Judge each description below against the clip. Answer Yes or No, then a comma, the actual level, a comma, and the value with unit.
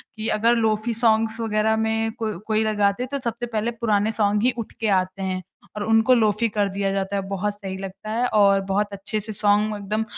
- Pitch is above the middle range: Yes, high, 215 Hz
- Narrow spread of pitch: Yes, narrow, 1.8 semitones